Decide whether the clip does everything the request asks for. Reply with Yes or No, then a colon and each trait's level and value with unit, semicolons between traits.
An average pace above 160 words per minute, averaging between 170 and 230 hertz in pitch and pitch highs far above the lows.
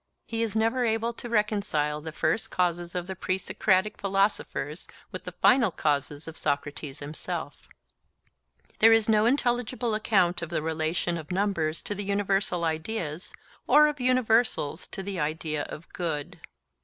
No: average, 155 wpm; medium, 185 Hz; wide, 5.7 semitones